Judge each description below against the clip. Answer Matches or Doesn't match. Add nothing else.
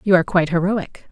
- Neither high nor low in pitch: Matches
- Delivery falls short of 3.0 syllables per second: Doesn't match